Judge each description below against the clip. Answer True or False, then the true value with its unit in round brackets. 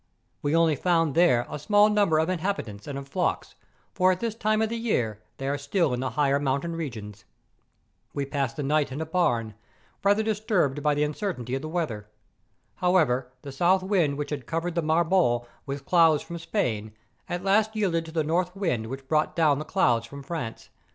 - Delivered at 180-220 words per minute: True (200 wpm)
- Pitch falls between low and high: True (155 Hz)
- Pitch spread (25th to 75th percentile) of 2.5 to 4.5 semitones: False (5.0 semitones)